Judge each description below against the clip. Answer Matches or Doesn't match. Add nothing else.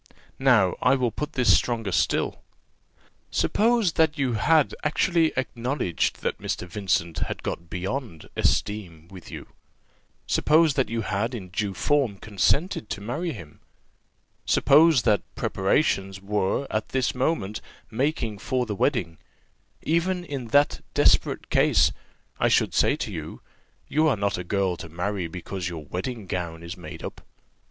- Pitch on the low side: Matches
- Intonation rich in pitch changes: Matches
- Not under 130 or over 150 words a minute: Matches